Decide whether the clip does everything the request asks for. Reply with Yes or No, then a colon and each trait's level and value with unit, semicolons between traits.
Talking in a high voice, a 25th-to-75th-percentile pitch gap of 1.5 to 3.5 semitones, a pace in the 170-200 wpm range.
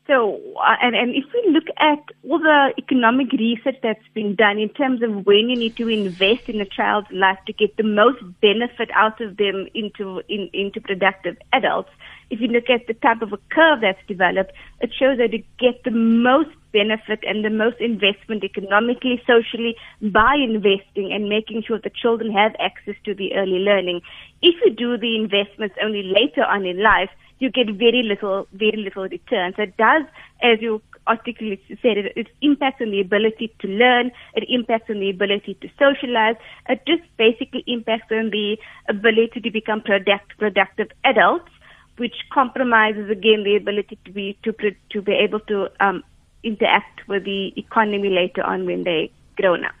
Yes: high, 220 Hz; average, 2.9 semitones; average, 180 wpm